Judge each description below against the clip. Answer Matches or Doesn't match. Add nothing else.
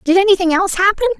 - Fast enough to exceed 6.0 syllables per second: Matches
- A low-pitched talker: Doesn't match